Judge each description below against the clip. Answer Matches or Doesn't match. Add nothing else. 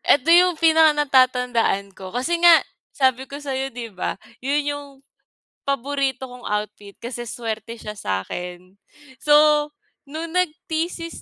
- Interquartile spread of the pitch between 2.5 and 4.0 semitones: Doesn't match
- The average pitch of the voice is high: Matches